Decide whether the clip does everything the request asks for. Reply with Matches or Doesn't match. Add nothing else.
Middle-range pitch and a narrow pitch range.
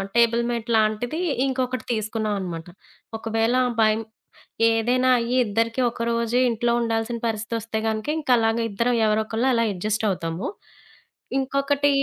Doesn't match